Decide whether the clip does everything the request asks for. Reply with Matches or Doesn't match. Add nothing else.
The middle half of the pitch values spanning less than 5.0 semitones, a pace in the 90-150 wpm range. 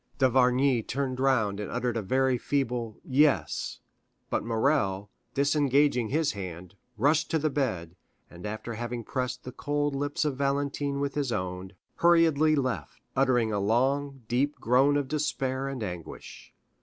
Matches